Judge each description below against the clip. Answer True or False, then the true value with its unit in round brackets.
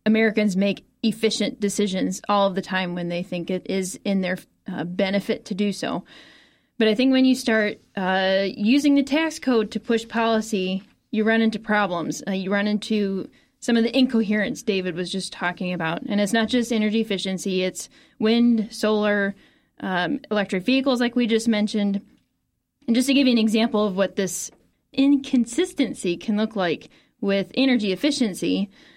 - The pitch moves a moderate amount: True (3.6 semitones)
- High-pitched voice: True (215 Hz)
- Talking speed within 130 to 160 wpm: False (175 wpm)